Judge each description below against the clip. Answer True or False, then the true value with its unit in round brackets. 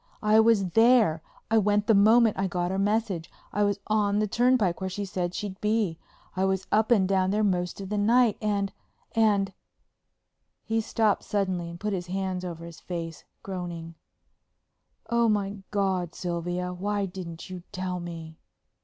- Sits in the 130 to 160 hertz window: False (195 Hz)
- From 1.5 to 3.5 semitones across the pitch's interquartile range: True (2.9 semitones)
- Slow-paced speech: False (160 wpm)